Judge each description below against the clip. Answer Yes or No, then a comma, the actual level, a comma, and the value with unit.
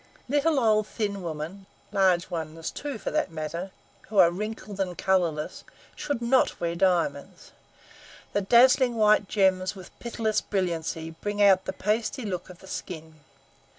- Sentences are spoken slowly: No, average, 150 wpm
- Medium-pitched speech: No, high, 195 Hz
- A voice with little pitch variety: No, average, 4.0 semitones